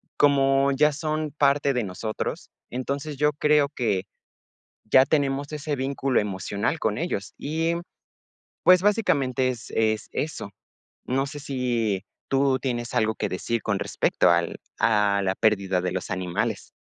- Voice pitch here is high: No, low, 130 Hz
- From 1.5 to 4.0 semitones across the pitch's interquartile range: No, average, 5.1 semitones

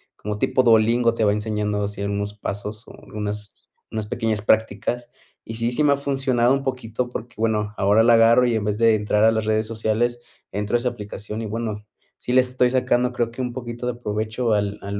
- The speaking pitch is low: Yes, low, 110 Hz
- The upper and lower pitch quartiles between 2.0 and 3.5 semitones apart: Yes, narrow, 2.5 semitones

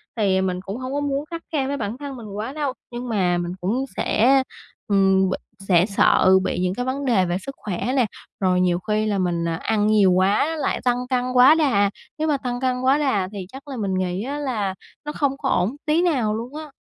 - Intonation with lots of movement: Yes, wide, 6.1 semitones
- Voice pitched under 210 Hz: No, high, 230 Hz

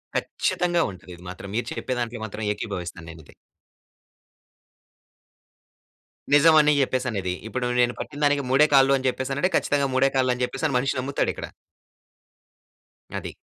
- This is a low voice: Yes, low, 130 Hz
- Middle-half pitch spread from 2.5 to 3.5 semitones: No, average, 4.2 semitones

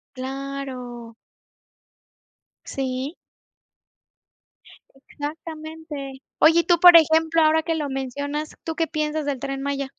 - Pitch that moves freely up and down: No, average, 2.9 semitones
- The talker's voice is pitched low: No, very high, 290 Hz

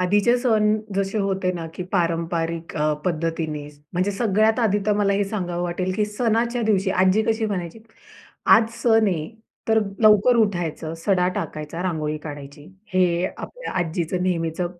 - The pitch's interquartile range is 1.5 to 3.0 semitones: No, average, 4.2 semitones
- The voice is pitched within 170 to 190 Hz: Yes, medium, 185 Hz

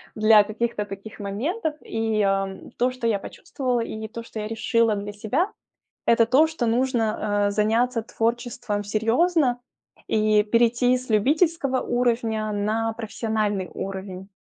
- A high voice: Yes, high, 225 Hz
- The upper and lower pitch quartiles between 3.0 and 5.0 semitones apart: No, narrow, 2.6 semitones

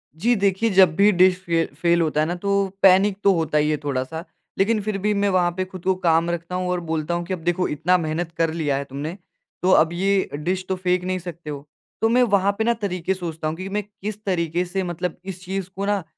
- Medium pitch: Yes, medium, 180 Hz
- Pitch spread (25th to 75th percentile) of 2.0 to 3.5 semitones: Yes, average, 2.9 semitones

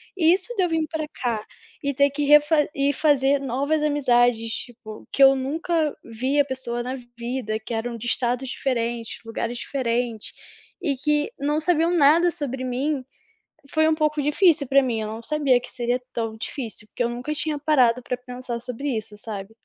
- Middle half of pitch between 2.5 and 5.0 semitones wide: Yes, average, 3.8 semitones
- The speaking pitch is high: Yes, very high, 265 Hz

